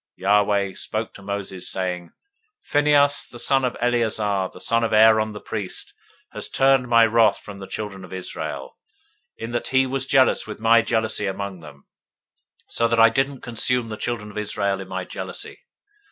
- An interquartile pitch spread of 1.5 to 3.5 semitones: Yes, average, 3.2 semitones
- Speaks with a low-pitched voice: Yes, low, 110 Hz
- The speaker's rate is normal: Yes, average, 185 wpm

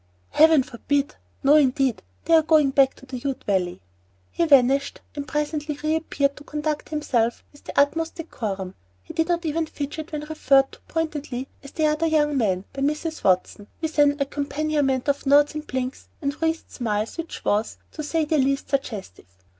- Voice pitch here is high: Yes, very high, 285 Hz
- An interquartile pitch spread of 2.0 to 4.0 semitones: Yes, average, 2.7 semitones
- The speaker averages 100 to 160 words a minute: No, average, 180 wpm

